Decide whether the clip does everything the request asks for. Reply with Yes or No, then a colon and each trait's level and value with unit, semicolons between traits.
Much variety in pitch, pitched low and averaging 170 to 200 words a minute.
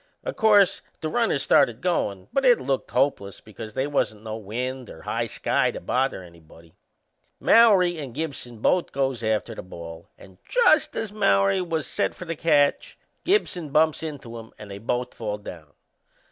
Yes: wide, 7.8 semitones; low, 130 Hz; average, 175 wpm